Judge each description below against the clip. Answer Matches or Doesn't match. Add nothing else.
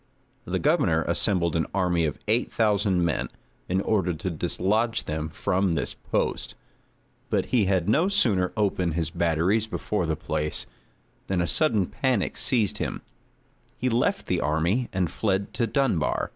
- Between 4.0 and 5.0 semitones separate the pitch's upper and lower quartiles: Matches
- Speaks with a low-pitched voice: Matches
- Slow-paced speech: Doesn't match